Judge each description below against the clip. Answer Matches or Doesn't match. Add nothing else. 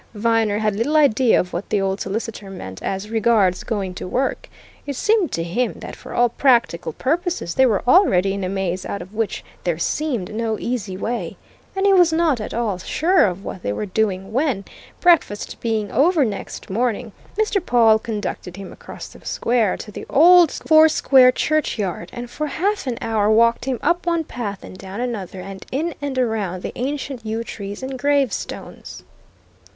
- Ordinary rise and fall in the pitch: Doesn't match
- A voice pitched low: Doesn't match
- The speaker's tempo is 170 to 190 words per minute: Matches